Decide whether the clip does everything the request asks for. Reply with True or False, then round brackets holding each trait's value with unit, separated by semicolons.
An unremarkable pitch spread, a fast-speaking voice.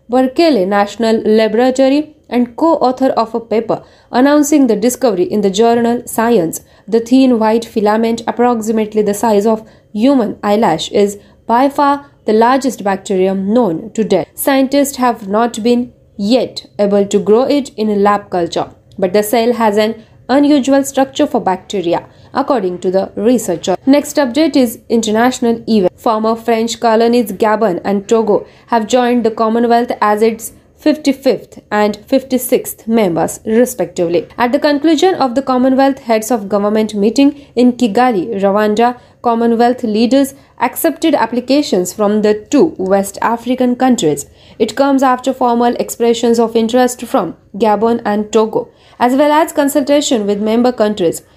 True (3.5 semitones; 145 wpm)